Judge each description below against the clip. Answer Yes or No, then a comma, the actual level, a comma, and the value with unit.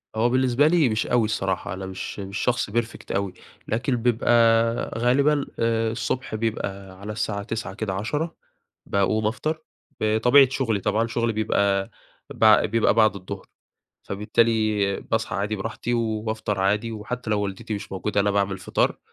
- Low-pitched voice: Yes, low, 110 Hz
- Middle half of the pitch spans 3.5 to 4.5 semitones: No, average, 2.7 semitones